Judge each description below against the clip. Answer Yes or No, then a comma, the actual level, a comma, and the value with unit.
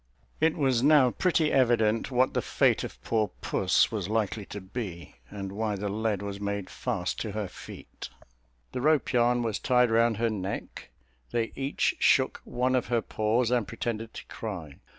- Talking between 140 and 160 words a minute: No, average, 175 wpm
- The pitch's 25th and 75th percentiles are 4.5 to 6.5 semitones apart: No, average, 3.4 semitones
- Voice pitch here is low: Yes, low, 115 Hz